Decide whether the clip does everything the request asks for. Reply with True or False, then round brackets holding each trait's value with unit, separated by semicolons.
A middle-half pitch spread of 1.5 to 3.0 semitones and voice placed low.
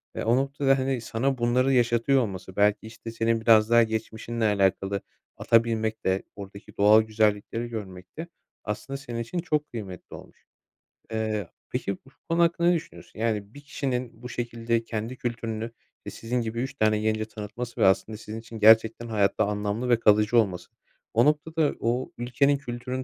True (2.5 semitones; 115 Hz)